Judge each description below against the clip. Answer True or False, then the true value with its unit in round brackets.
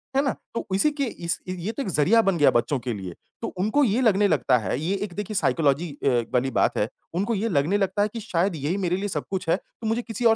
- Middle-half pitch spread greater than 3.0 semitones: True (5.3 semitones)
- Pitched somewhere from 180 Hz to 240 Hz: True (190 Hz)